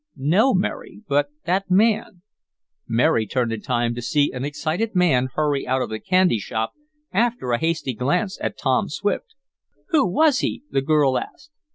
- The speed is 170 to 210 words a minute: Yes, average, 175 wpm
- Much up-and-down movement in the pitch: Yes, wide, 7.3 semitones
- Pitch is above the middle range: No, medium, 155 Hz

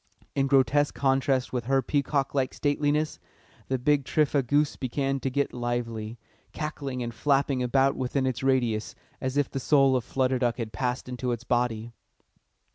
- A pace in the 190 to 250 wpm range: No, average, 165 wpm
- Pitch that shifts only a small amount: Yes, narrow, 2.2 semitones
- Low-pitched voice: Yes, low, 130 Hz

